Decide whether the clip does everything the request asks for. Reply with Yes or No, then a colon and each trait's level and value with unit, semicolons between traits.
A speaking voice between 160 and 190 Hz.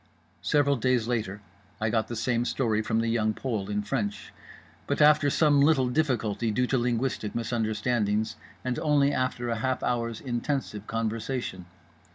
No: low, 120 Hz